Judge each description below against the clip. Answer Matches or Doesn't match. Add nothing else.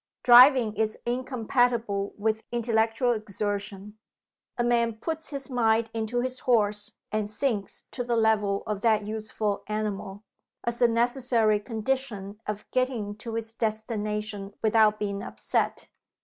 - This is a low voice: Doesn't match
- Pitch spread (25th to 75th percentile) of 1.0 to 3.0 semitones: Matches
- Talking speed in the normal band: Doesn't match